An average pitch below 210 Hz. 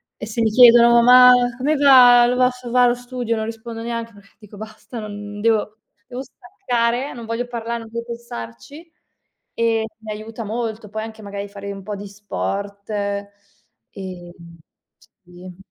No: high, 225 Hz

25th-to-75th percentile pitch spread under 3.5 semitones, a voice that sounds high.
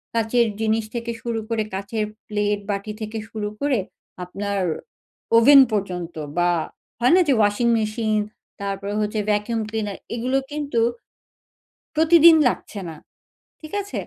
Yes: narrow, 2.6 semitones; high, 220 Hz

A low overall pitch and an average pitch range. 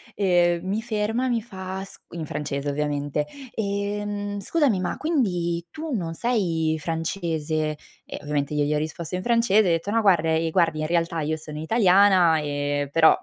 No: medium, 170 Hz; average, 4.6 semitones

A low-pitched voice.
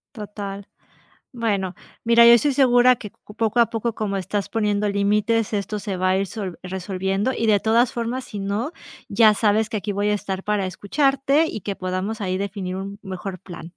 No: high, 210 Hz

